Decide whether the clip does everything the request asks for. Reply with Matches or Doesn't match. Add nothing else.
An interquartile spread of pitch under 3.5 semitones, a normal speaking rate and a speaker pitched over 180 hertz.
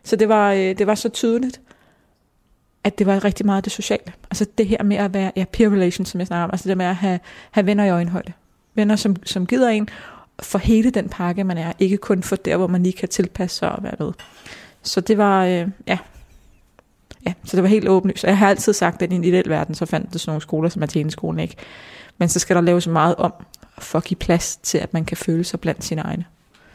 Doesn't match